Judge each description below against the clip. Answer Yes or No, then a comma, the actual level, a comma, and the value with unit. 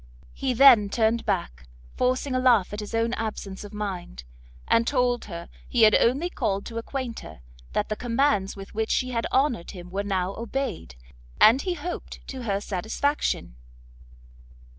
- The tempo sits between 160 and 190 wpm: Yes, average, 165 wpm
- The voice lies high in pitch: Yes, high, 225 Hz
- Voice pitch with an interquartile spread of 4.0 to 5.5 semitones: Yes, average, 4.4 semitones